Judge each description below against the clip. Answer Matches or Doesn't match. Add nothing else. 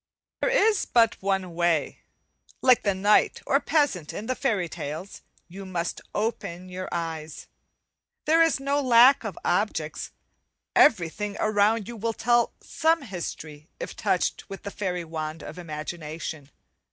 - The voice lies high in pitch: Matches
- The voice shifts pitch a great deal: Matches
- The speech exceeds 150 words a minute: Doesn't match